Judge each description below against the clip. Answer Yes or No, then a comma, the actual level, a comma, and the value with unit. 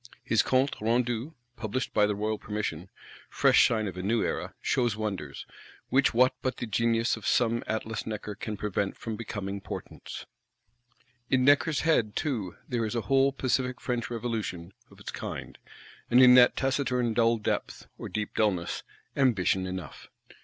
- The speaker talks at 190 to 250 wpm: No, average, 160 wpm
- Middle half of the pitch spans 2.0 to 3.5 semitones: Yes, average, 3.2 semitones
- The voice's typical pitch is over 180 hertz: No, low, 115 Hz